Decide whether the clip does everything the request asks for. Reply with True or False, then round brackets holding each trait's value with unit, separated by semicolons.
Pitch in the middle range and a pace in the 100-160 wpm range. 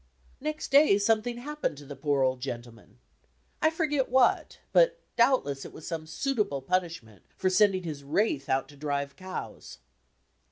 True (180 Hz; 155 wpm)